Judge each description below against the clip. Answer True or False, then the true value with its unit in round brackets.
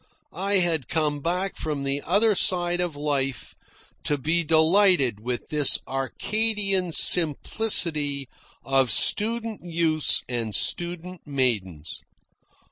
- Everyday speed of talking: False (110 wpm)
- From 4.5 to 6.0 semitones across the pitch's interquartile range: True (4.8 semitones)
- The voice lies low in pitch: False (160 Hz)